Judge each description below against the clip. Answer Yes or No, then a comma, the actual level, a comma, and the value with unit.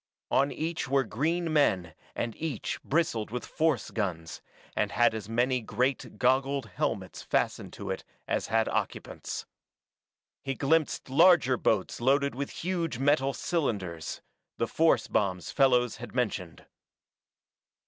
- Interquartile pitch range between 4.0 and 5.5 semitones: Yes, average, 4.5 semitones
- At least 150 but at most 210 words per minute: No, slow, 135 wpm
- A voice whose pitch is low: Yes, low, 130 Hz